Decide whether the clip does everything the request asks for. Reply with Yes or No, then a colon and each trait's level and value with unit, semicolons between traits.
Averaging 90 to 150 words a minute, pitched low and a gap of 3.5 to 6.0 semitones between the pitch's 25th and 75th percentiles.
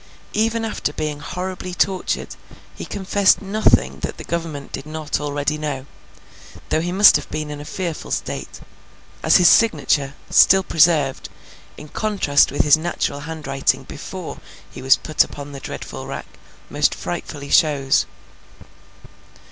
No: average, 140 wpm; medium, 155 Hz; average, 4.2 semitones